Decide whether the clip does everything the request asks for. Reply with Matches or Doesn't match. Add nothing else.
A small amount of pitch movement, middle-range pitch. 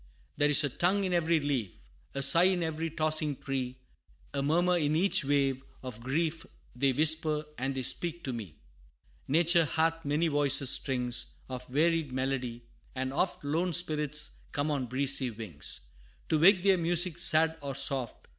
Doesn't match